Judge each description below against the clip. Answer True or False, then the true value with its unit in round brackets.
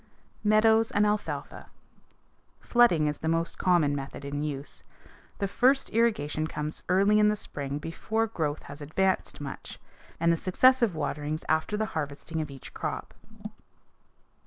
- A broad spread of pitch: True (6.2 semitones)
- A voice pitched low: False (165 Hz)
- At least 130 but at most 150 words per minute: True (140 wpm)